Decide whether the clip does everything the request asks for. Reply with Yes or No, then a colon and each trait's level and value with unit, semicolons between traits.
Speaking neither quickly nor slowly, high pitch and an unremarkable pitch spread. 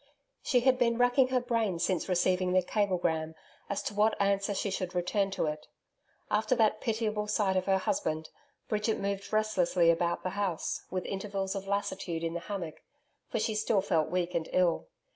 Yes: average, 180 wpm; high, 195 Hz; average, 3.1 semitones